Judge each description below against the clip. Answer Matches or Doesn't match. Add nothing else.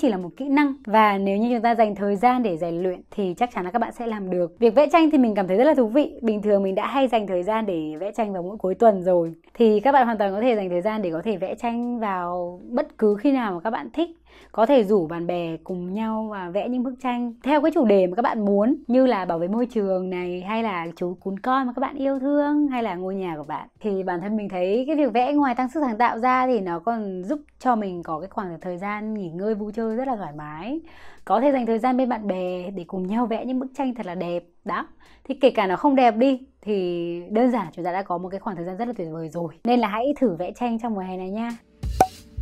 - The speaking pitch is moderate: Doesn't match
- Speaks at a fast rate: Matches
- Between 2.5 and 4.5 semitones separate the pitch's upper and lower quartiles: Doesn't match